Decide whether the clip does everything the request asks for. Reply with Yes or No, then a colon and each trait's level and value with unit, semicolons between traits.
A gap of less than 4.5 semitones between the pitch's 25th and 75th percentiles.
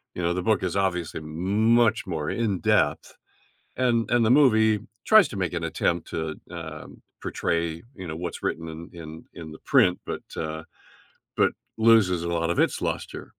No: average, 4.9 semitones